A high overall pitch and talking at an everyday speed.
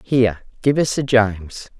No: low, 115 Hz; average, 170 wpm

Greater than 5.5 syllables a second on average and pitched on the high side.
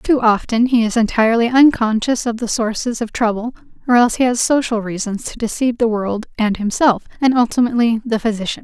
Yes: 5.9 syllables/s; high, 230 Hz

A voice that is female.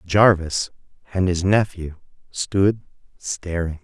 No: male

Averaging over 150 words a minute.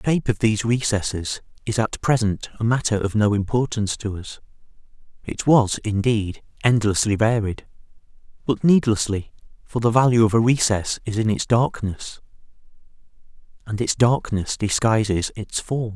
No: average, 145 wpm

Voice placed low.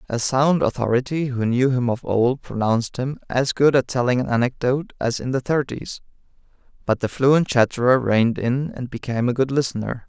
Yes: low, 125 Hz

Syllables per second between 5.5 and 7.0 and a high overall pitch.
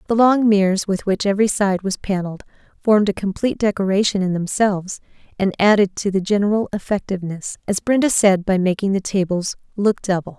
Yes: 5.9 syllables/s; high, 200 Hz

